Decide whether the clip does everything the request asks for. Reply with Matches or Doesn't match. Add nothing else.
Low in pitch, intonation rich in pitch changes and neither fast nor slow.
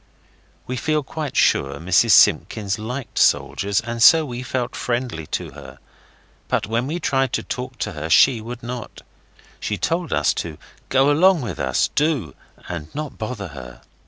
Matches